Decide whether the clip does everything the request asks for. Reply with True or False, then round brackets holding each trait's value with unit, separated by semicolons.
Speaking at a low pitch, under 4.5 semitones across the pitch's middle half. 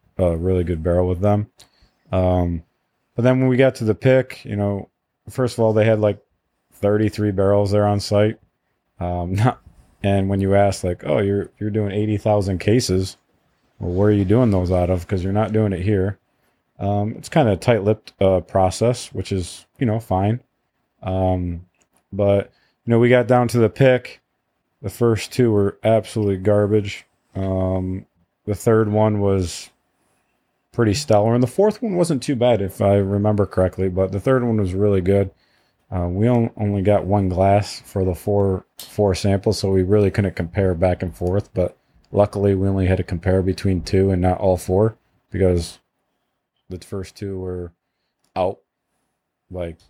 True (100 Hz; 2.7 semitones)